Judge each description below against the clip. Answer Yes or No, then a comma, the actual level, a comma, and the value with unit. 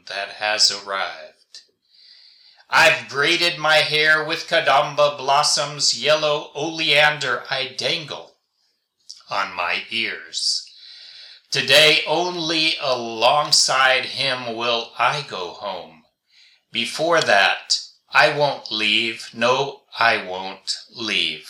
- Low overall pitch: No, medium, 145 Hz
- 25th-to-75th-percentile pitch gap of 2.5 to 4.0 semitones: No, average, 5.0 semitones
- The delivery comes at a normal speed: No, slow, 95 wpm